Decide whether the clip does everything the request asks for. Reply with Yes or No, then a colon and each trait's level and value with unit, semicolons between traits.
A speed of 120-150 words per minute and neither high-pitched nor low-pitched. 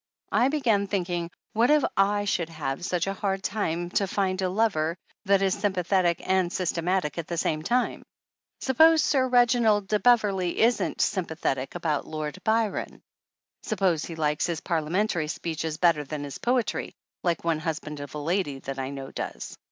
No: average, 175 wpm; medium, 180 Hz